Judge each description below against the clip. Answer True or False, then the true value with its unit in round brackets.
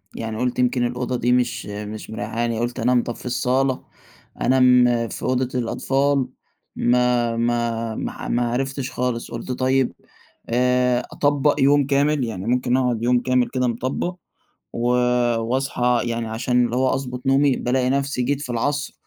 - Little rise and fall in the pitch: True (1.8 semitones)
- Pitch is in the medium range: False (125 Hz)